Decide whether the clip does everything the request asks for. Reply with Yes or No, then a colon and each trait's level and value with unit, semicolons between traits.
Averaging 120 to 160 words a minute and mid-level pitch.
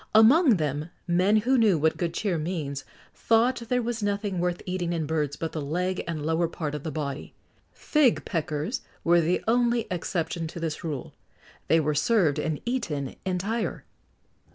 No: average, 175 wpm; medium, 175 Hz